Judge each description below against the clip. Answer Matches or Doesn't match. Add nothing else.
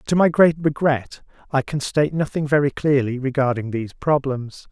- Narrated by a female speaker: Doesn't match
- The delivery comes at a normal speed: Matches